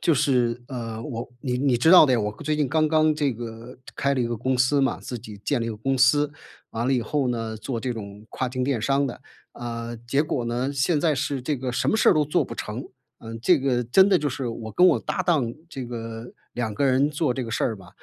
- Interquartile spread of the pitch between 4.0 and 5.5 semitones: No, average, 3.5 semitones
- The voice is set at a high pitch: No, low, 125 Hz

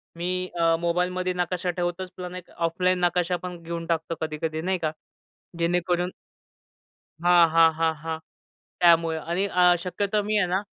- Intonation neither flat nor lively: No, narrow, 1.6 semitones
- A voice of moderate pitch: Yes, medium, 175 Hz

